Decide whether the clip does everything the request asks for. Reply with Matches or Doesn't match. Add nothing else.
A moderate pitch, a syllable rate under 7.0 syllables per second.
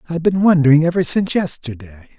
Doesn't match